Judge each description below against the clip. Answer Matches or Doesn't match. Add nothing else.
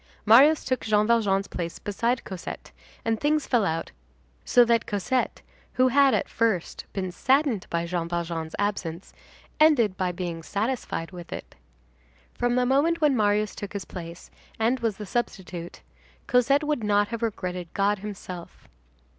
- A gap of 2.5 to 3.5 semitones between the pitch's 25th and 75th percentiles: Doesn't match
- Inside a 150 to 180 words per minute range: Matches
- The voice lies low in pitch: Doesn't match